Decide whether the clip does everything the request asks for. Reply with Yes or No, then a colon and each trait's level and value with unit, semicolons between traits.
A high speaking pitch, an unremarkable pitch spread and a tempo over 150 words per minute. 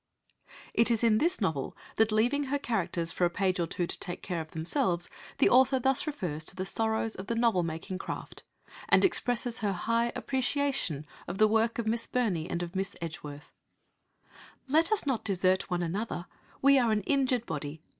No: high, 215 Hz; wide, 5.8 semitones; average, 190 wpm